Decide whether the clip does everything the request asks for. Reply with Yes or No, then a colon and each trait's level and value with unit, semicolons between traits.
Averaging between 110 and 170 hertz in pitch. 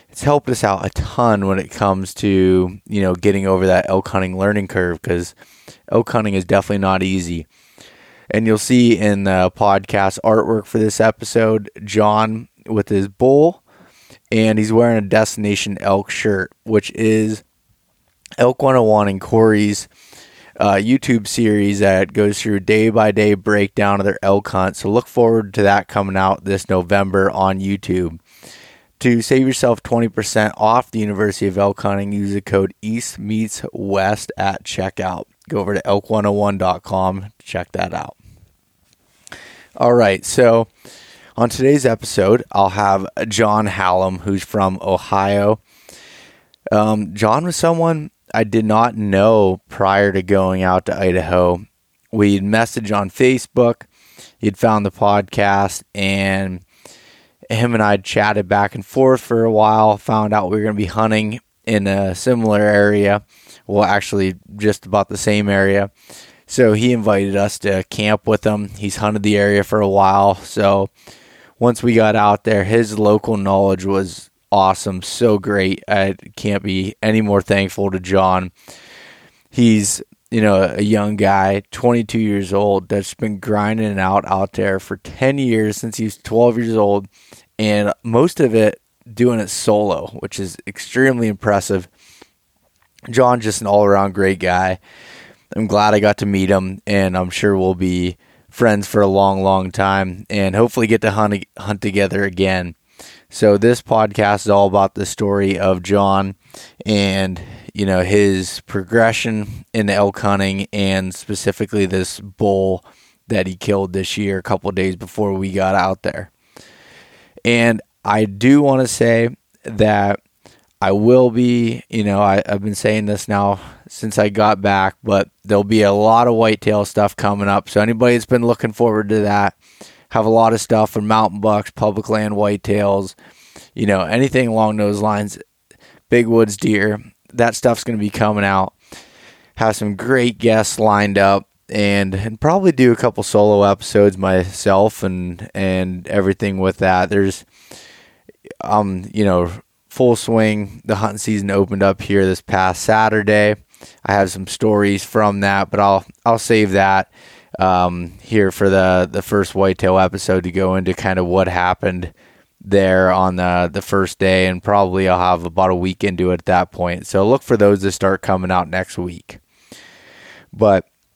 No: low, 100 Hz